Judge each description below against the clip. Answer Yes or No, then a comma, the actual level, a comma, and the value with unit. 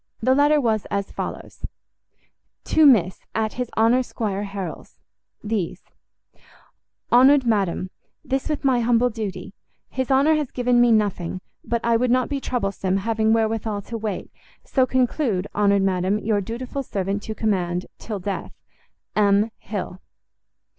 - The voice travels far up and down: No, average, 3.9 semitones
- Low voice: No, high, 220 Hz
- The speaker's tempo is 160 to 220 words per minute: No, average, 140 wpm